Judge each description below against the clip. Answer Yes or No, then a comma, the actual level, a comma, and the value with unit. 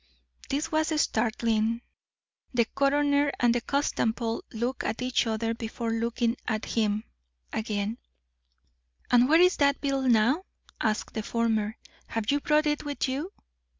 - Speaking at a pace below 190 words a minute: Yes, average, 140 wpm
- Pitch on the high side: Yes, high, 240 Hz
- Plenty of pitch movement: No, average, 4.1 semitones